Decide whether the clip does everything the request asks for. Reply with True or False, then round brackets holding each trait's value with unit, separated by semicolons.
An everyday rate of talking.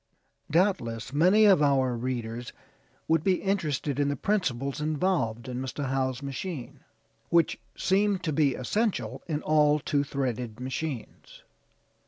False (130 wpm)